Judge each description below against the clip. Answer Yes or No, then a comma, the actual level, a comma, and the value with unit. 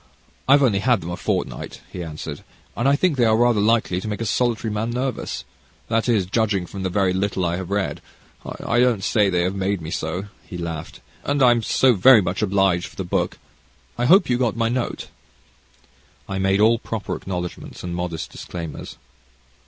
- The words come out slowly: No, average, 200 wpm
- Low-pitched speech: Yes, low, 100 Hz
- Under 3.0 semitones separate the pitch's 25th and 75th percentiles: No, average, 4.6 semitones